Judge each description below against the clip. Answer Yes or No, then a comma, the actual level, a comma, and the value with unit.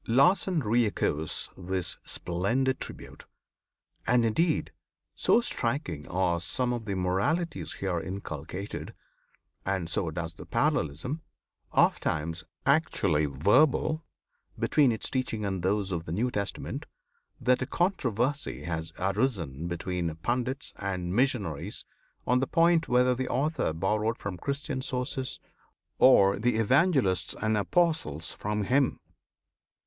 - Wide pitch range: Yes, wide, 6.6 semitones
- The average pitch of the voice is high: No, low, 105 Hz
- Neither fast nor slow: No, slow, 120 wpm